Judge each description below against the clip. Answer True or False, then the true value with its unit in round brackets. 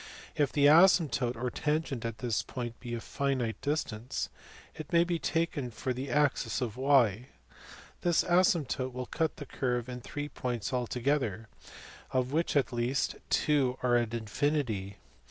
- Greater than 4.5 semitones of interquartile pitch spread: False (3.6 semitones)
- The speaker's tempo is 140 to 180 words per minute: True (160 wpm)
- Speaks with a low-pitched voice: True (130 Hz)